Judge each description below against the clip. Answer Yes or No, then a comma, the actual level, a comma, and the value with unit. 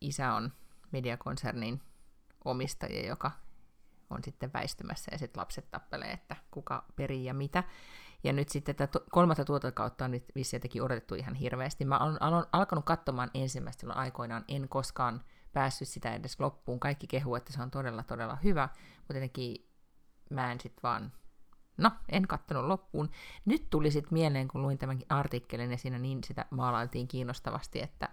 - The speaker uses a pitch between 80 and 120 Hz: No, low, 135 Hz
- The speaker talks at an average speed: No, fast, 160 wpm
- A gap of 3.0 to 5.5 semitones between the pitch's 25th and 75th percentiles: No, narrow, 2.5 semitones